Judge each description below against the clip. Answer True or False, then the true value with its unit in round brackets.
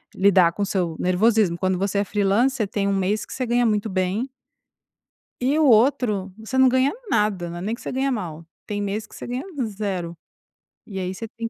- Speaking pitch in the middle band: False (205 Hz)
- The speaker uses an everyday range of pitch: True (3.8 semitones)